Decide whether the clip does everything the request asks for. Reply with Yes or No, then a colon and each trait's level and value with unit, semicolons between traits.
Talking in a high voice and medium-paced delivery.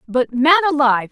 Yes: very high, 275 Hz; average, 160 wpm